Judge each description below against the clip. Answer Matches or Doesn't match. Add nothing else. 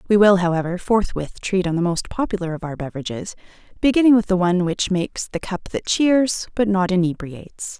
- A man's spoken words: Doesn't match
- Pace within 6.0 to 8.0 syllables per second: Doesn't match